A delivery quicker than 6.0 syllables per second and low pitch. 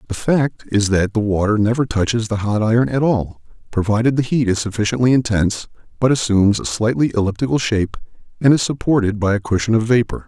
Yes: 6.2 syllables/s; low, 110 Hz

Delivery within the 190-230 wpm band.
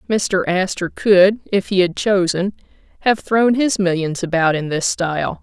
No: average, 165 wpm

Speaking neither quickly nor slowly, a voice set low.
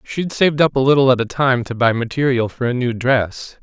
No: fast, 250 wpm; low, 130 Hz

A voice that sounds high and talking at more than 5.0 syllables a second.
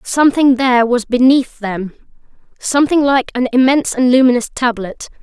Yes: very high, 250 Hz; 5.2 syllables/s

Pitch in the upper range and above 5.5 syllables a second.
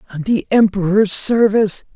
No: high, 200 Hz; 5.2 syllables/s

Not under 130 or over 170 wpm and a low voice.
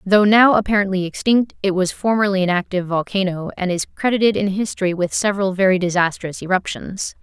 No: average, 165 wpm; high, 195 Hz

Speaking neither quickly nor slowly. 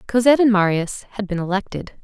Yes: average, 175 wpm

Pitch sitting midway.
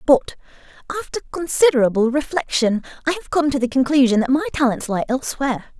No: very high, 275 Hz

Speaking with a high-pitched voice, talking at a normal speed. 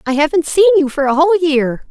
No: very high, 300 Hz; fast, 250 wpm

